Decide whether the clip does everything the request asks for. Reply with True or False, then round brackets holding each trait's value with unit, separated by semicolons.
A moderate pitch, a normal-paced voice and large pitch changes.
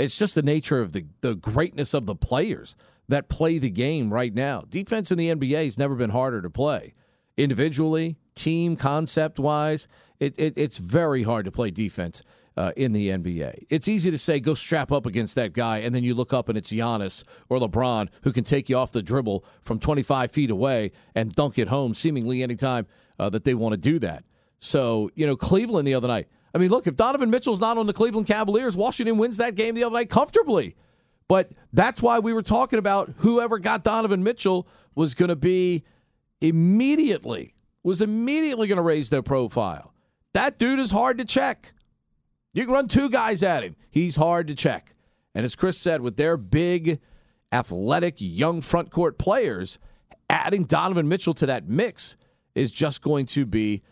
True (155 Hz; 195 wpm; 7.1 semitones)